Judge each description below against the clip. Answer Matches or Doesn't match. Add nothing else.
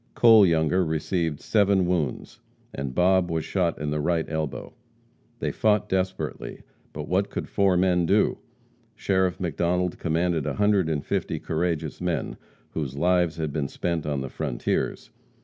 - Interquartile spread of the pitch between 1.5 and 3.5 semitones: Matches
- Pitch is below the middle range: Matches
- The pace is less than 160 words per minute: Matches